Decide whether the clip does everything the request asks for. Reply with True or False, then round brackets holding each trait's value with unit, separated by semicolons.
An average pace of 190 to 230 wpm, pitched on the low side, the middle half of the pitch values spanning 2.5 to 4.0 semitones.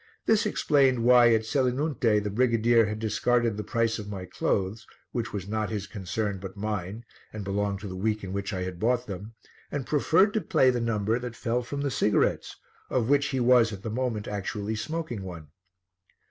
True (195 wpm; 110 Hz; 3.4 semitones)